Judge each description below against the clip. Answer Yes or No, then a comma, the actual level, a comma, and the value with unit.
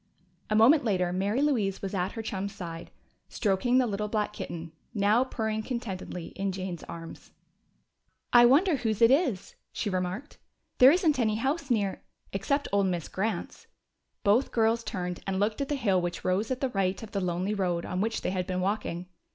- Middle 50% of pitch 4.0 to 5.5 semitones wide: Yes, average, 4.4 semitones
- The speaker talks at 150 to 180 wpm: No, average, 190 wpm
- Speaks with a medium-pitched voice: No, high, 205 Hz